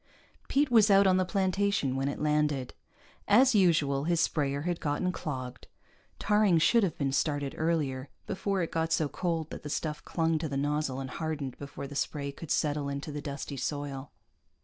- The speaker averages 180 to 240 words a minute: Yes, average, 185 wpm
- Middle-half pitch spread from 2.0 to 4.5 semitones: Yes, average, 4.1 semitones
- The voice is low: No, medium, 150 Hz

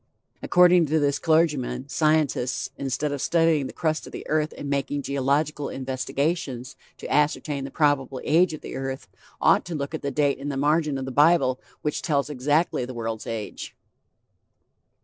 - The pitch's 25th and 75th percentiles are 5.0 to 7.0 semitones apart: No, narrow, 2.6 semitones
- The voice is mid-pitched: Yes, medium, 145 Hz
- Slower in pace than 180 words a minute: Yes, average, 170 wpm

